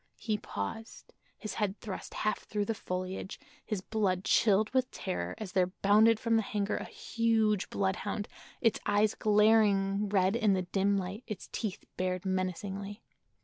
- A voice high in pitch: Yes, high, 205 Hz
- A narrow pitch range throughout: Yes, narrow, 2.3 semitones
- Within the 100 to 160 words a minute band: Yes, average, 155 wpm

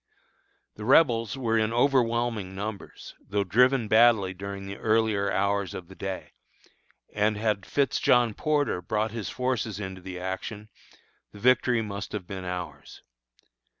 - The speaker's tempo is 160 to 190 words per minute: No, average, 145 wpm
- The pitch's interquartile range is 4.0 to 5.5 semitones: No, average, 3.2 semitones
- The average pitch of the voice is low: Yes, low, 105 Hz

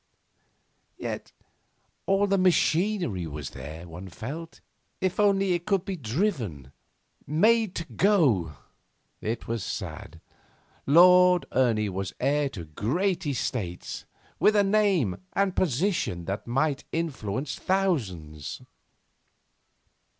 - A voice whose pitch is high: No, medium, 145 Hz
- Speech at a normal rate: No, slow, 105 wpm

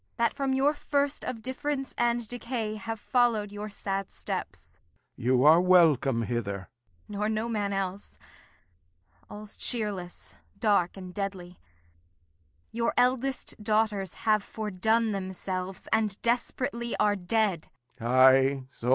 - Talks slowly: Yes, slow, 115 wpm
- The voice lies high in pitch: Yes, high, 210 Hz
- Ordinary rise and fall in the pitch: Yes, average, 4.0 semitones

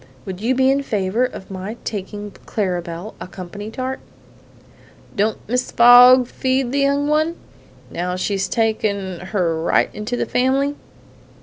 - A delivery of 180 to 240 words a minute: No, average, 145 wpm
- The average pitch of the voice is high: Yes, high, 220 Hz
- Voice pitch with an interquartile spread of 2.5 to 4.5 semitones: No, average, 5.3 semitones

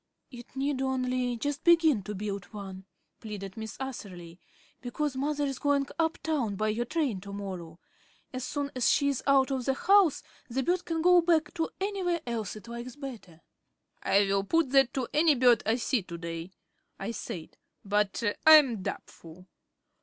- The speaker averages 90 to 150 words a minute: No, average, 170 wpm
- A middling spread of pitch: No, wide, 6.1 semitones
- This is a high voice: Yes, very high, 250 Hz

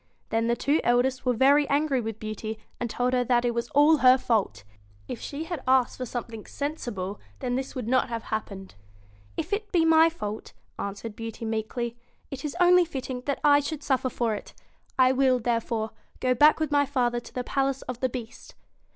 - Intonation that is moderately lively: Yes, average, 3.6 semitones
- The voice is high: Yes, very high, 250 Hz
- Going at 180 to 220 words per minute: Yes, average, 200 wpm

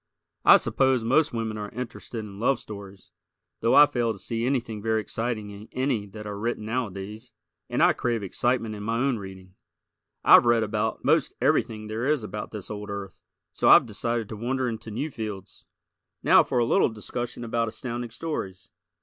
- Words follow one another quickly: No, average, 180 wpm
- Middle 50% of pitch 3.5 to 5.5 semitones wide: No, narrow, 2.5 semitones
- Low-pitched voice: Yes, low, 110 Hz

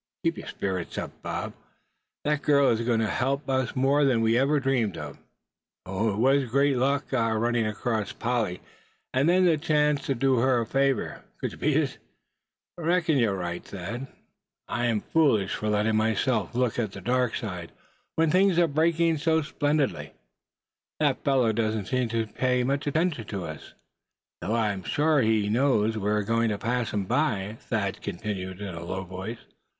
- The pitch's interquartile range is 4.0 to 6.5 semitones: Yes, average, 4.8 semitones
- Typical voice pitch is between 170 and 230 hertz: No, low, 120 Hz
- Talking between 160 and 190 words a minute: Yes, average, 180 wpm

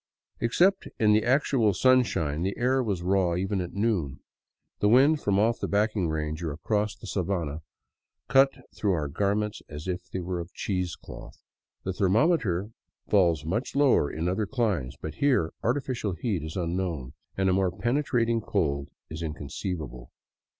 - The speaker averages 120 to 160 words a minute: Yes, average, 155 wpm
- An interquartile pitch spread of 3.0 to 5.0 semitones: No, wide, 5.4 semitones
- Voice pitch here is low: Yes, very low, 95 Hz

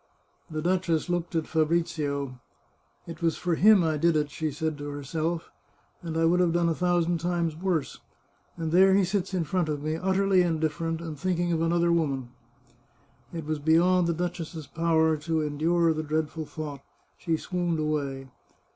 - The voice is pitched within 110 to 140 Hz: No, medium, 165 Hz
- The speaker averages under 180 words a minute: No, average, 185 wpm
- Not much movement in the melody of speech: Yes, narrow, 2.0 semitones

